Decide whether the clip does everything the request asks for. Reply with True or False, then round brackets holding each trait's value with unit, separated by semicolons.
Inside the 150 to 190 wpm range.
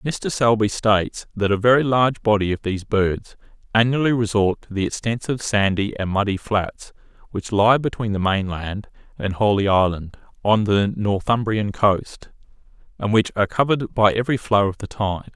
True (165 wpm)